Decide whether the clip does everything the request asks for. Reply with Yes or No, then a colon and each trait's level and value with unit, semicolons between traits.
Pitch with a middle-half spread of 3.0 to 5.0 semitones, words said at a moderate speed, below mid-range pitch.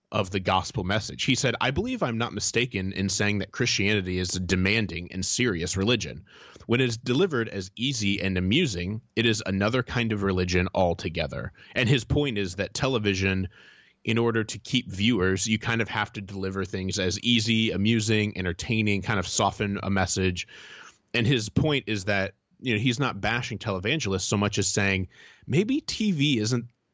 Yes: average, 3.6 semitones; average, 180 wpm; low, 105 Hz